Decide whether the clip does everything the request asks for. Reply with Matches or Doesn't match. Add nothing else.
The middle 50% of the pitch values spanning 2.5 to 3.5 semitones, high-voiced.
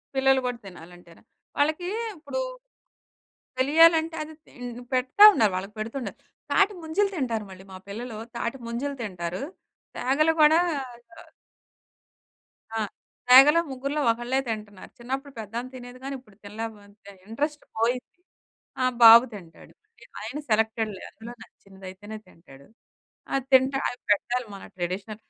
Doesn't match